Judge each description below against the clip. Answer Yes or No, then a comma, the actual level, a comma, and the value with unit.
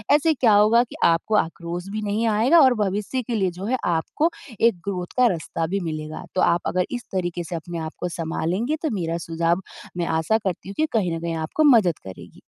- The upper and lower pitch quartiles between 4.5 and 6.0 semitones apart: Yes, average, 4.8 semitones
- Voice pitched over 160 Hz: Yes, medium, 185 Hz